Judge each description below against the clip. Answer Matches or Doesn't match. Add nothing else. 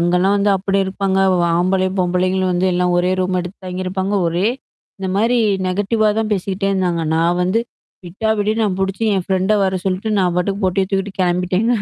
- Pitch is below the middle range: Doesn't match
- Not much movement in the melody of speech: Matches